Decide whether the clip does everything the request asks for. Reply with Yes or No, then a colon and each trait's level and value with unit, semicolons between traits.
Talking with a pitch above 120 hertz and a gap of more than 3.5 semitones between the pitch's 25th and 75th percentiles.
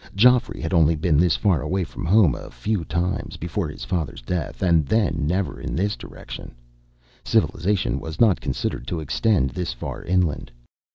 No: very low, 85 Hz; average, 3.9 semitones